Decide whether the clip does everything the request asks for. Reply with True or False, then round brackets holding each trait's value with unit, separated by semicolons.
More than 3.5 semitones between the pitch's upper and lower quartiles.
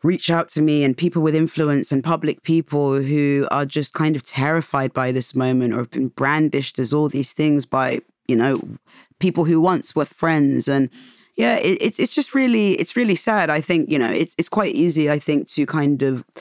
False (3.1 semitones)